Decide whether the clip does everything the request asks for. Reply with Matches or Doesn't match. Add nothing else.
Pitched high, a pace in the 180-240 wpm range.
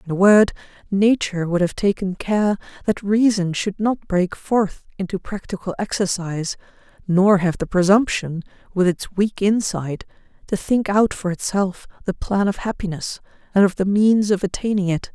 Doesn't match